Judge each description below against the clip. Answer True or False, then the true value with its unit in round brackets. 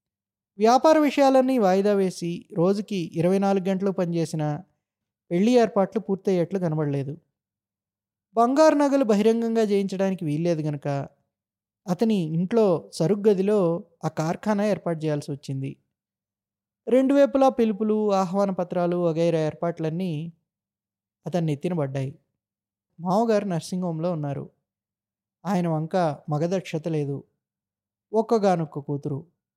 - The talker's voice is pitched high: False (170 Hz)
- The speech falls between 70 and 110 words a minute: True (95 wpm)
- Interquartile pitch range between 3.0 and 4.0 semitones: False (5.6 semitones)